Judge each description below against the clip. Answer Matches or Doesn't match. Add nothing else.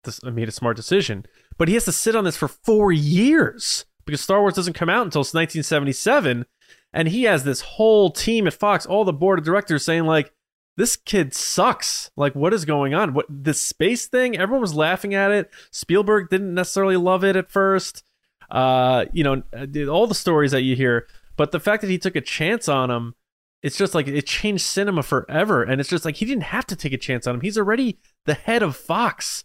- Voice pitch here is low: Doesn't match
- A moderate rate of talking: Doesn't match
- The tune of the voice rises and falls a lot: Matches